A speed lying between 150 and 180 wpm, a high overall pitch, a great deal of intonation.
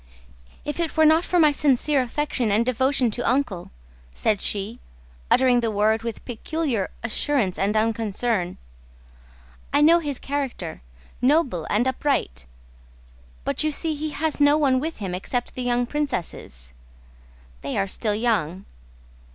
No: average, 140 wpm; high, 245 Hz; wide, 5.8 semitones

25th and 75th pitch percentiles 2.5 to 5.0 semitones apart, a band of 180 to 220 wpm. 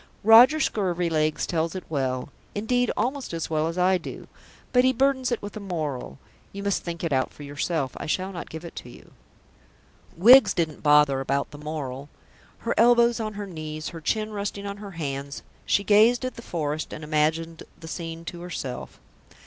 No: wide, 5.6 semitones; average, 190 wpm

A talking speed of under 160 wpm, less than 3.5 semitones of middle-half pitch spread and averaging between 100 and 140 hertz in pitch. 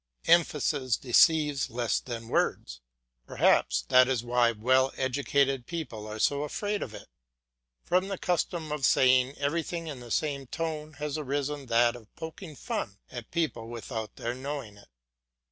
No: average, 150 wpm; average, 4.2 semitones; low, 135 Hz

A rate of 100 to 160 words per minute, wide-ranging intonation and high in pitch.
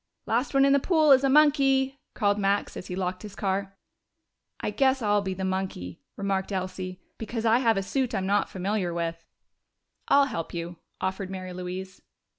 No: average, 185 wpm; wide, 5.7 semitones; high, 195 Hz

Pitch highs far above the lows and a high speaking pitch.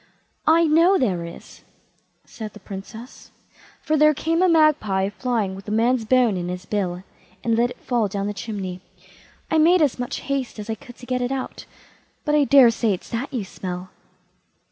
Yes: wide, 5.9 semitones; high, 235 Hz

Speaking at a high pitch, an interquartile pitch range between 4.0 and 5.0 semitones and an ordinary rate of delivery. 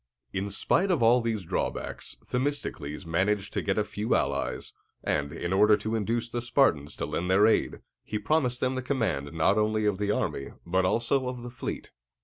No: low, 105 Hz; average, 4.4 semitones; average, 190 wpm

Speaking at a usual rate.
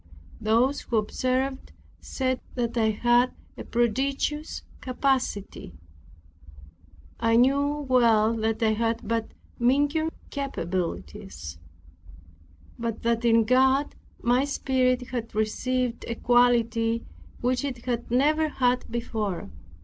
No: slow, 105 wpm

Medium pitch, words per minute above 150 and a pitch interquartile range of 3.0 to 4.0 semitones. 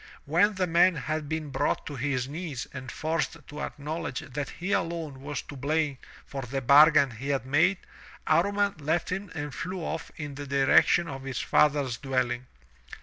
Yes: medium, 150 Hz; average, 175 wpm; average, 3.4 semitones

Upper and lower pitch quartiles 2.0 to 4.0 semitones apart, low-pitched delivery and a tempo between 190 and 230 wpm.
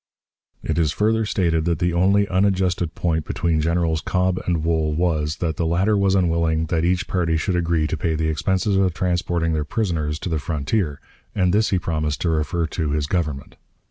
Yes: narrow, 2.6 semitones; very low, 85 Hz; average, 195 wpm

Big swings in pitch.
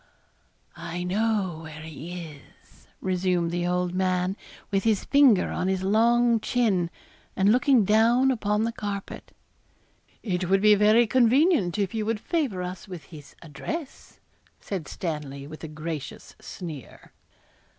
No: average, 4.4 semitones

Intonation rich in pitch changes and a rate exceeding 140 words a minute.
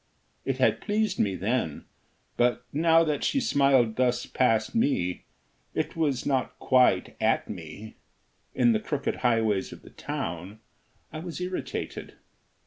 No: wide, 6.3 semitones; slow, 135 wpm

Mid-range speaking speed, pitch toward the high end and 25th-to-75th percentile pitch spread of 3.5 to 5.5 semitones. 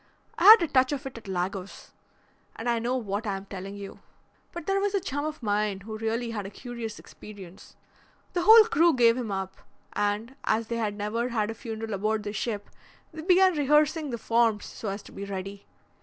No: fast, 210 wpm; high, 225 Hz; average, 5.1 semitones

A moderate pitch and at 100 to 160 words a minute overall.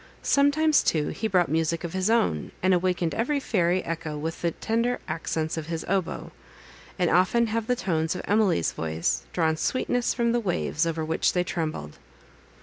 No: medium, 180 Hz; average, 175 wpm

